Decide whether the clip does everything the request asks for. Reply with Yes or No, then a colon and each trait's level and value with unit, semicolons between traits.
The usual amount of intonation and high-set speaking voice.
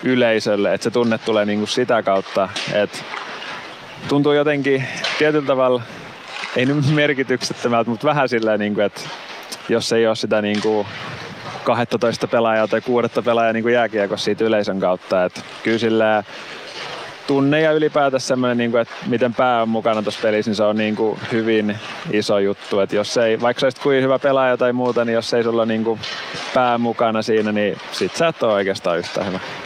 No: average, 3.3 semitones; low, 115 Hz